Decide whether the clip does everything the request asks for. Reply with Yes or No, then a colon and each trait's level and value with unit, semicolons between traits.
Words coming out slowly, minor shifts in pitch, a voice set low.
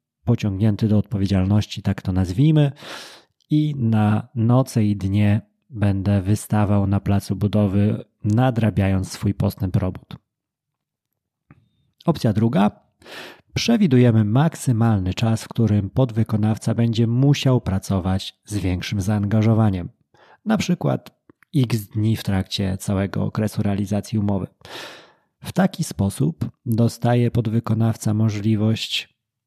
No: slow, 100 wpm; average, 3.0 semitones; low, 110 Hz